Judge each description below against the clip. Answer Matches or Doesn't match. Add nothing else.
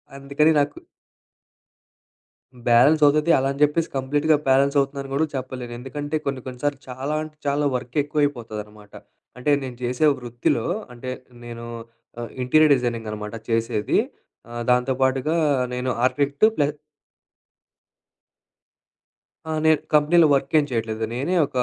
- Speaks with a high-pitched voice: Doesn't match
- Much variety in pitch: Doesn't match